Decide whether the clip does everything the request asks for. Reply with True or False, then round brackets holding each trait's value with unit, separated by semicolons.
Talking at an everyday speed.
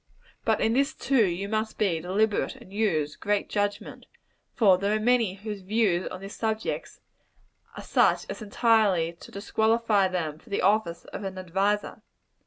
True (165 wpm)